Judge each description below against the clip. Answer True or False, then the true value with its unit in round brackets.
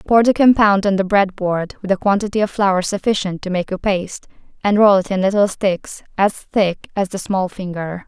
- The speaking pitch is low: False (195 Hz)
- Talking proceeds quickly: True (215 wpm)